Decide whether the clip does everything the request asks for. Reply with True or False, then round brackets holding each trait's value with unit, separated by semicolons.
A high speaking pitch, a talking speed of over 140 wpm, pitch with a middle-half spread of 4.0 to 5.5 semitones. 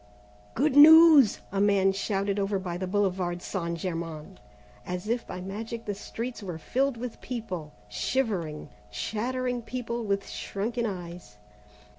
False (200 Hz; 135 wpm; 4.8 semitones)